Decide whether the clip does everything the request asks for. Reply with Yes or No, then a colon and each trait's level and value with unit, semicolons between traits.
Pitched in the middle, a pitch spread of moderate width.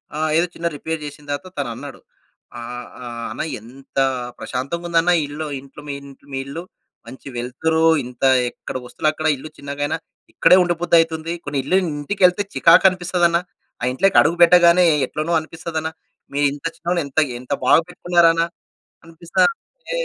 Yes: medium, 160 Hz; average, 3.4 semitones